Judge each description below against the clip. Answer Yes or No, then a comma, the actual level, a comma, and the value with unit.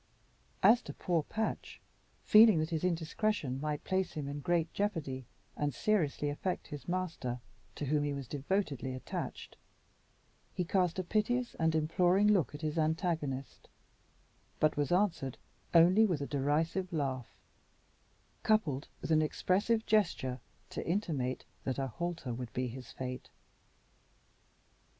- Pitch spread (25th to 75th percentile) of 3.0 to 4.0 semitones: No, average, 4.9 semitones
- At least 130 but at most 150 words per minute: Yes, slow, 135 wpm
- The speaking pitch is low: No, medium, 160 Hz